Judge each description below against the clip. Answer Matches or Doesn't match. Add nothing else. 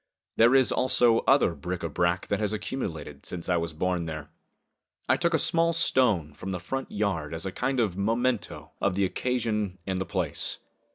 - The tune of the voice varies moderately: Doesn't match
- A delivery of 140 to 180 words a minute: Doesn't match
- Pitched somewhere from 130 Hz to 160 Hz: Doesn't match